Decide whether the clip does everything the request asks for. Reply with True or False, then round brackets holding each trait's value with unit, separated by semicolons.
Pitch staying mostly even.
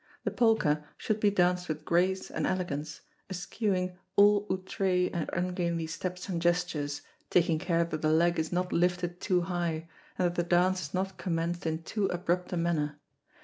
True (1.7 semitones)